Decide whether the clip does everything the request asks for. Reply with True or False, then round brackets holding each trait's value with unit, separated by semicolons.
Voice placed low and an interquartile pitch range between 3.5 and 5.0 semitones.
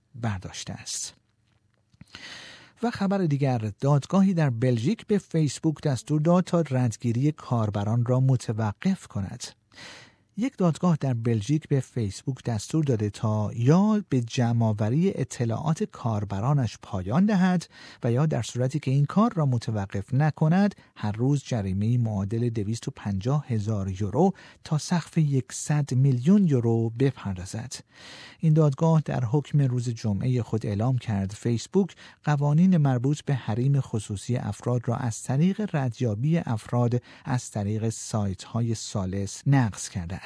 False (125 Hz; 5.4 semitones)